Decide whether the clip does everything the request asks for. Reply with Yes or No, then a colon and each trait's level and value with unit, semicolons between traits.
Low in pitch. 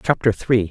Yes: low, 110 Hz